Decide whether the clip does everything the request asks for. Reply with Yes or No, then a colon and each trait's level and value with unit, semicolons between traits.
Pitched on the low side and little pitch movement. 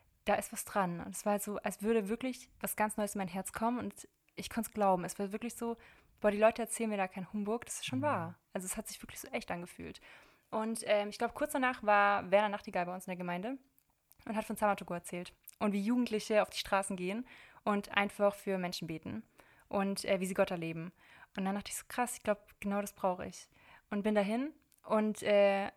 No: high, 205 Hz; narrow, 2.1 semitones